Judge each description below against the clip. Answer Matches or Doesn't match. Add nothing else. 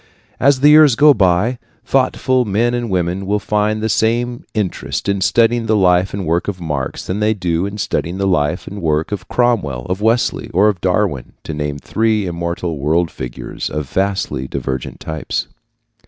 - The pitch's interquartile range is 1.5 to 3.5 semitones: Doesn't match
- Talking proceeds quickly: Doesn't match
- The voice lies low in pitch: Matches